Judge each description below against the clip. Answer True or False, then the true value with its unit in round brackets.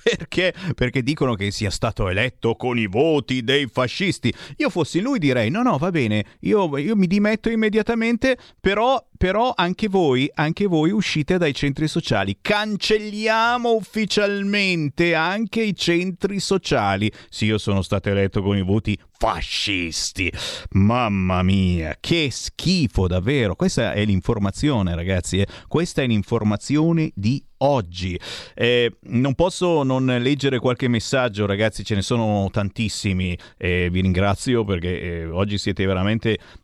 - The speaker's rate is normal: True (140 wpm)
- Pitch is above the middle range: False (125 Hz)